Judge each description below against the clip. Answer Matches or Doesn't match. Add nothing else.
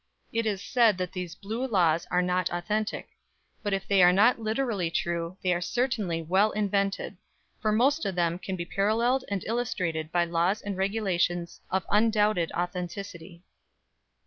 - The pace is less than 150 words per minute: Doesn't match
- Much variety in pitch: Doesn't match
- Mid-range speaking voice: Doesn't match